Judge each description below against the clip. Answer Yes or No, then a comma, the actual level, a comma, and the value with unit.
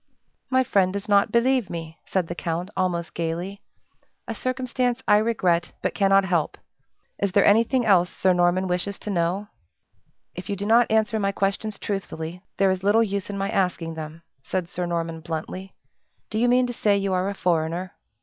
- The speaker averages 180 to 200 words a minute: Yes, average, 185 wpm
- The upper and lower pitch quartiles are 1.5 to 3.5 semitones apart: Yes, average, 3.2 semitones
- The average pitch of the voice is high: Yes, high, 195 Hz